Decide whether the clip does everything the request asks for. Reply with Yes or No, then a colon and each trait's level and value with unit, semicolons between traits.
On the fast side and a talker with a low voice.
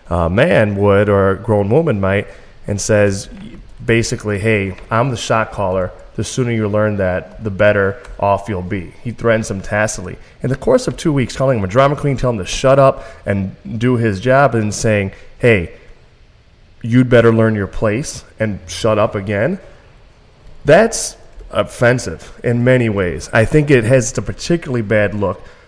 No: average, 175 wpm; low, 110 Hz